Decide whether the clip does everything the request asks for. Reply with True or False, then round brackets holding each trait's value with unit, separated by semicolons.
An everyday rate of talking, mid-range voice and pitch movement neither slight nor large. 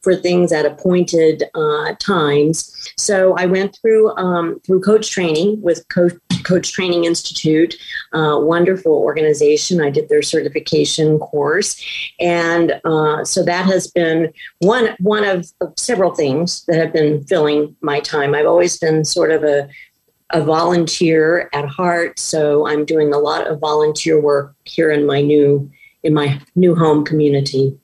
True (155 wpm; 165 Hz; 3.3 semitones)